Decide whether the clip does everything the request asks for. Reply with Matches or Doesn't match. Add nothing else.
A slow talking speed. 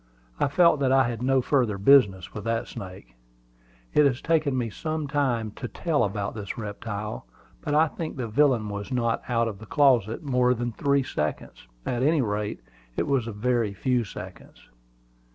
Doesn't match